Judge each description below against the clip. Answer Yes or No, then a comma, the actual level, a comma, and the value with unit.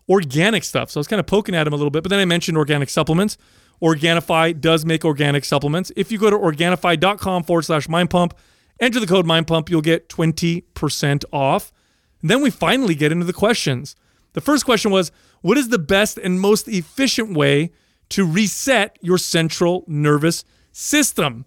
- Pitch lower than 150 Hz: No, medium, 175 Hz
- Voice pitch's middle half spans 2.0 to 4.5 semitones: Yes, average, 3.7 semitones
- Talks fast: No, average, 190 wpm